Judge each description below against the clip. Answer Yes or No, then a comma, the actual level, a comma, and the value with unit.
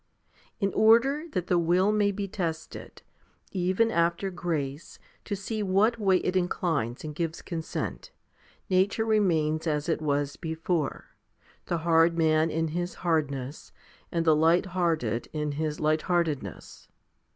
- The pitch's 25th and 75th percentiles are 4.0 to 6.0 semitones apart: No, average, 3.3 semitones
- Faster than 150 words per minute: No, average, 140 wpm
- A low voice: No, medium, 170 Hz